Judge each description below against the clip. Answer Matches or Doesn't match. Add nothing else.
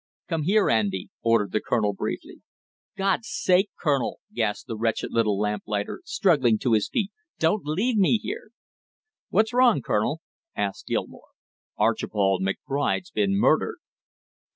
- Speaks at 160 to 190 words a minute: Doesn't match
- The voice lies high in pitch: Doesn't match